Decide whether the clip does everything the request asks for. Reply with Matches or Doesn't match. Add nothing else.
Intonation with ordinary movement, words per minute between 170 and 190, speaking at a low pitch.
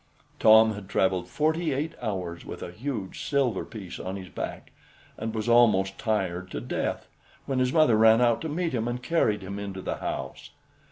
Matches